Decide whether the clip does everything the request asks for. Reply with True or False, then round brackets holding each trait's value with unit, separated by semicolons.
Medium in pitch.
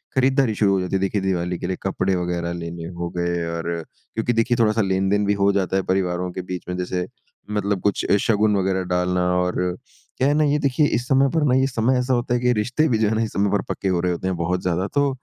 False (95 Hz)